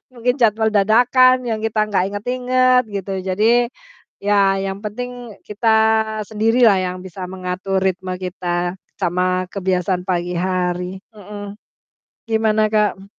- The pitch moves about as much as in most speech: Yes, average, 3.3 semitones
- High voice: Yes, high, 205 Hz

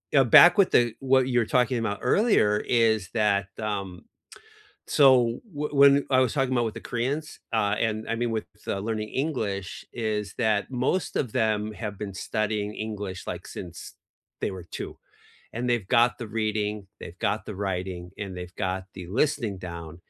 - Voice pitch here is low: Yes, low, 110 Hz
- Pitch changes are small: No, average, 3.7 semitones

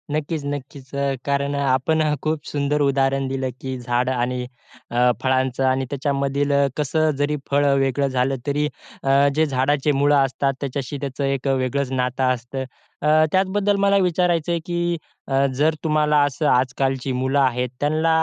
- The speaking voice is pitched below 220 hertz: Yes, medium, 140 Hz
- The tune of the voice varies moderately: No, narrow, 2.2 semitones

